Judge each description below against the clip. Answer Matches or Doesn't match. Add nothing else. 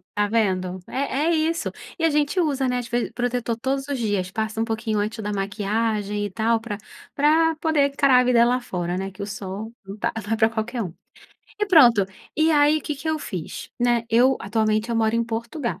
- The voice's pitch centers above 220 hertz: Matches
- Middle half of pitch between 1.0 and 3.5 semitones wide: Doesn't match